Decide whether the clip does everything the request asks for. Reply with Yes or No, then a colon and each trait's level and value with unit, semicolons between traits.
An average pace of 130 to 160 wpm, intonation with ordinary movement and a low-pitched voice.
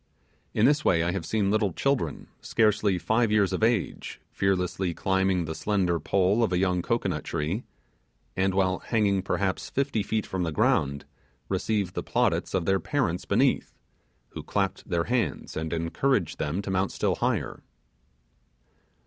Yes: average, 155 wpm; average, 3.6 semitones; very low, 95 Hz